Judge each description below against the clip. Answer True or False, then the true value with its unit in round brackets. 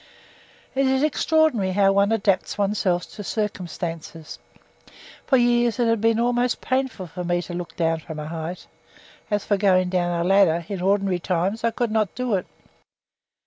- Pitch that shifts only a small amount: False (4.5 semitones)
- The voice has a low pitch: False (195 Hz)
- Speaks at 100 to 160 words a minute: False (170 wpm)